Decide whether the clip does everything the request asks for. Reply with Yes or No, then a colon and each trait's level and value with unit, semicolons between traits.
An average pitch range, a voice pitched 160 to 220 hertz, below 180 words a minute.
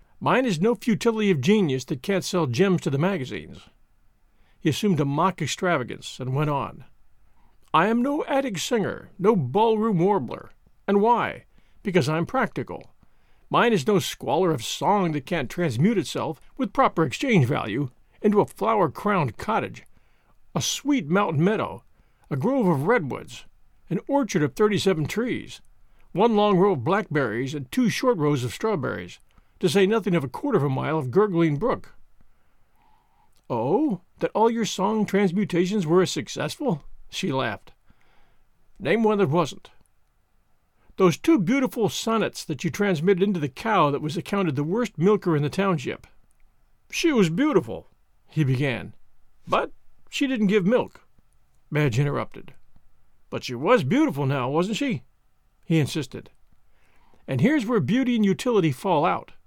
No: wide, 5.8 semitones; high, 190 Hz; average, 155 wpm